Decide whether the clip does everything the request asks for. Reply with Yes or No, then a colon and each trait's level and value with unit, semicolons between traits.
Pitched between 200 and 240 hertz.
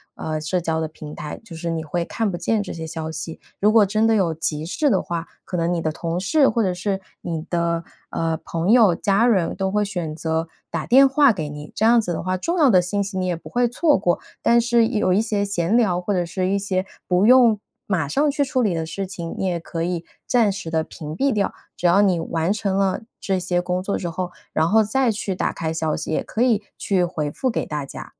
No: medium, 185 Hz